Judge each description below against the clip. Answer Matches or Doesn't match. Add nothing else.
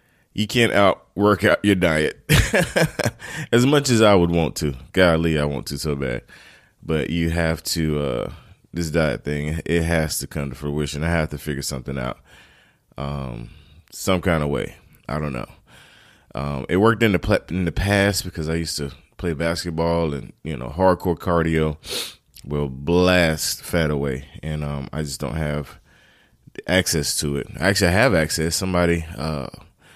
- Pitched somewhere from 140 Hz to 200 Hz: Doesn't match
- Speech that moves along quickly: Doesn't match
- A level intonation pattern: Doesn't match